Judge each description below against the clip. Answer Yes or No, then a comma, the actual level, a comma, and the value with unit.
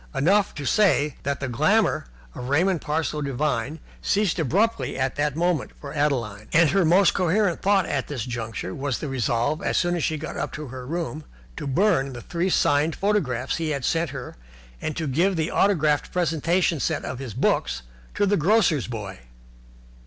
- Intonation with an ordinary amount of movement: Yes, average, 4.7 semitones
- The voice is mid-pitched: Yes, medium, 150 Hz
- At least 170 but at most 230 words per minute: Yes, average, 180 wpm